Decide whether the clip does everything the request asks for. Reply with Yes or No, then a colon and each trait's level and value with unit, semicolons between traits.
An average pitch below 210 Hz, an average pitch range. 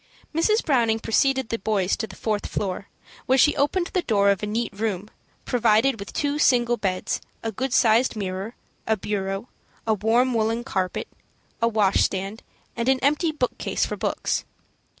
No: high, 225 Hz; average, 4.2 semitones